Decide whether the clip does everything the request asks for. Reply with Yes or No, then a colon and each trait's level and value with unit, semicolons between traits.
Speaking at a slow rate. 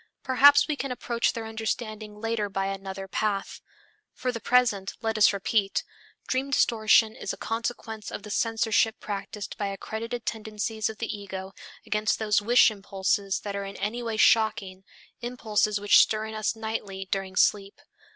No: average, 160 wpm